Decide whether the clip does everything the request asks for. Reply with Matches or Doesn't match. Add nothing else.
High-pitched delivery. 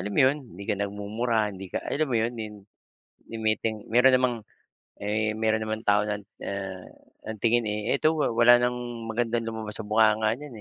Doesn't match